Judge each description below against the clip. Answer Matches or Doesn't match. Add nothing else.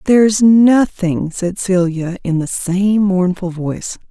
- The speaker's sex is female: Matches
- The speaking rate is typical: Doesn't match